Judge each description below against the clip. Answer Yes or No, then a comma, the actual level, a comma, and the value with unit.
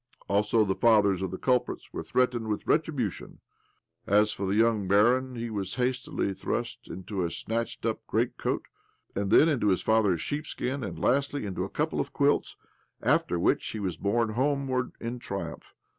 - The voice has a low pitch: Yes, low, 110 Hz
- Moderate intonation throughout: Yes, average, 4.2 semitones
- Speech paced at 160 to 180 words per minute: Yes, average, 165 wpm